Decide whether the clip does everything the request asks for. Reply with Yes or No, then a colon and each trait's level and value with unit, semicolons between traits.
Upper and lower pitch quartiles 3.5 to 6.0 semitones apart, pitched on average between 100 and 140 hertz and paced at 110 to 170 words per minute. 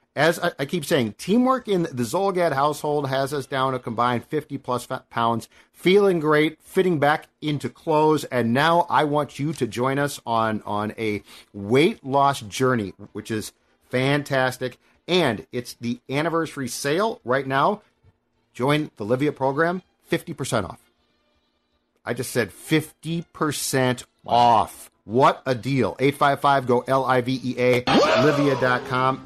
Yes: average, 3.9 semitones; low, 135 Hz; average, 145 wpm